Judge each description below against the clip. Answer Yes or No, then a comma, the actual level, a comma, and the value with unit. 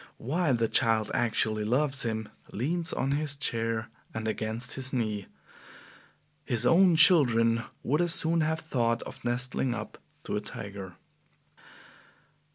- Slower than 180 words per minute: Yes, slow, 135 wpm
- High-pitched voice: No, low, 120 Hz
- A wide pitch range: No, average, 4.7 semitones